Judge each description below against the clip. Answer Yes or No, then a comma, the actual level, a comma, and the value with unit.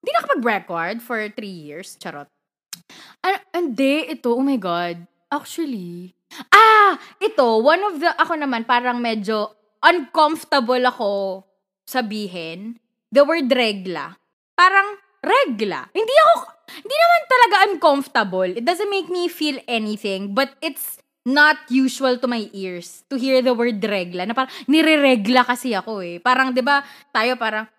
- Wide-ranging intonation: Yes, wide, 6.9 semitones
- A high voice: Yes, very high, 255 Hz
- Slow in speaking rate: No, average, 145 wpm